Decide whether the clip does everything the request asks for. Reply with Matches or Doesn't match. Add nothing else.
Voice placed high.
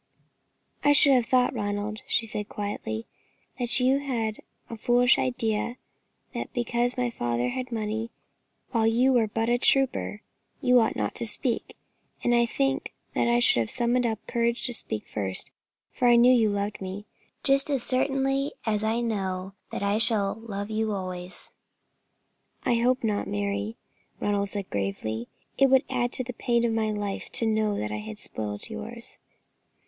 Matches